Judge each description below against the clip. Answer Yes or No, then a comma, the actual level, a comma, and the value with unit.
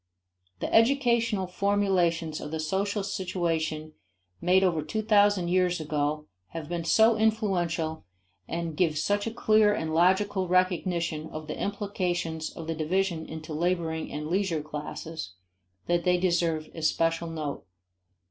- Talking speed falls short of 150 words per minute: Yes, slow, 135 wpm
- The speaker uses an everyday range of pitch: Yes, average, 3.5 semitones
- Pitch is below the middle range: No, medium, 175 Hz